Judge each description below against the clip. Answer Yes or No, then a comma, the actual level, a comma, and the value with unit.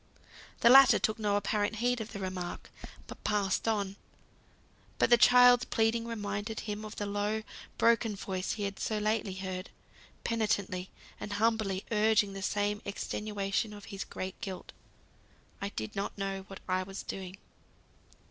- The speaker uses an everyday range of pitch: No, narrow, 2.1 semitones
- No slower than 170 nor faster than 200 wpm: No, average, 155 wpm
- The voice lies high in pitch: Yes, high, 205 Hz